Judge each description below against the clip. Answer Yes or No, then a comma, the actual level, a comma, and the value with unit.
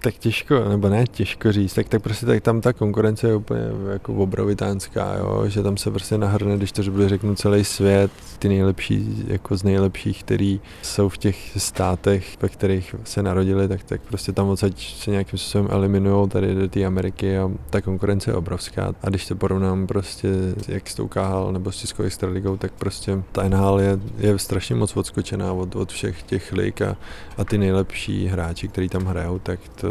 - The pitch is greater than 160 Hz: No, low, 100 Hz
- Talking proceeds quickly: Yes, fast, 195 wpm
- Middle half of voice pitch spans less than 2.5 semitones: Yes, narrow, 1.4 semitones